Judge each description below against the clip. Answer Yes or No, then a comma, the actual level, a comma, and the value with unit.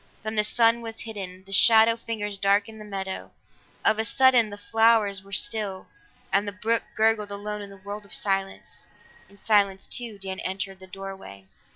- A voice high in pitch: Yes, high, 205 Hz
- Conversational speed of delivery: Yes, average, 180 wpm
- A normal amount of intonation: No, narrow, 2.2 semitones